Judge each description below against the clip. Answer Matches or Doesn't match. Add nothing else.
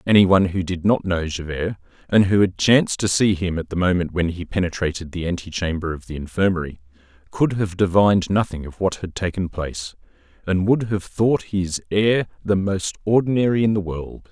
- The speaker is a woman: Doesn't match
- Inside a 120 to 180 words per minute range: Doesn't match